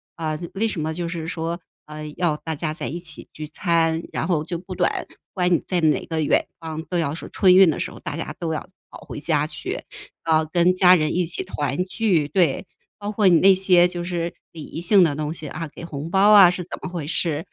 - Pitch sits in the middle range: Yes, medium, 170 Hz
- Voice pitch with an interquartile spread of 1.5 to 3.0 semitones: Yes, narrow, 2.4 semitones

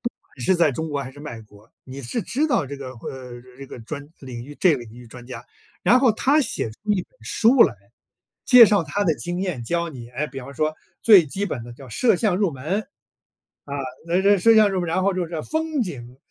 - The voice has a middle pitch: Yes, medium, 155 Hz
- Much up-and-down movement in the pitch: Yes, wide, 7.6 semitones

